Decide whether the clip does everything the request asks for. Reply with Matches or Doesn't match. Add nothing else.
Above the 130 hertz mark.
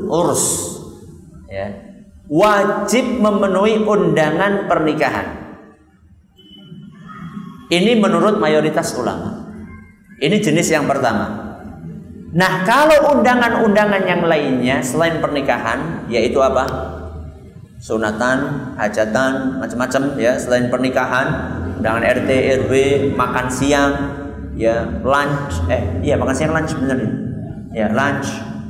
Matches